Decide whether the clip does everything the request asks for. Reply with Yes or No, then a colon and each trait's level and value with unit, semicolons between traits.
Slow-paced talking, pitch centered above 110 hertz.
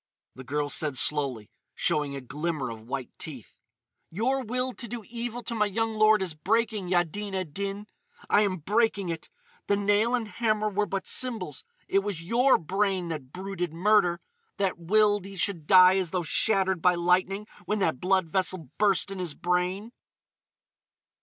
No: average, 165 wpm; high, 190 Hz